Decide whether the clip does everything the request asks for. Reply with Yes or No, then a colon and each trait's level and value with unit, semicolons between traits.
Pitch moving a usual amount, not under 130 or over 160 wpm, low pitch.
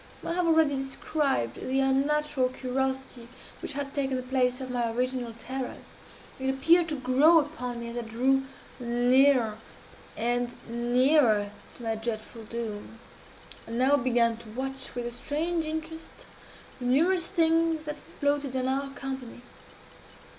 No: average, 3.1 semitones; average, 145 wpm; very high, 260 Hz